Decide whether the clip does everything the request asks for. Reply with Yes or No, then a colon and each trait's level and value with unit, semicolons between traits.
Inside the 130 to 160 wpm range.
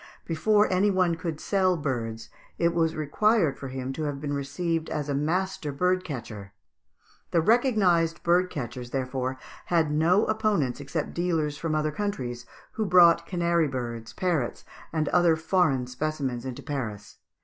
Yes: average, 150 wpm